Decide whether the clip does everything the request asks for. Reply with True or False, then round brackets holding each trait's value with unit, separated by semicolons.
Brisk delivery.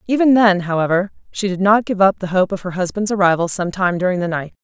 True (235 wpm)